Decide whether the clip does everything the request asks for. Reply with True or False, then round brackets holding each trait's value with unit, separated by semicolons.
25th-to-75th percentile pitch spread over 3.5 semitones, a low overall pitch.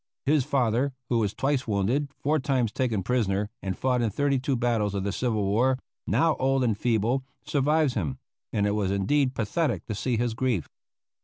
True (4.5 semitones; 120 Hz)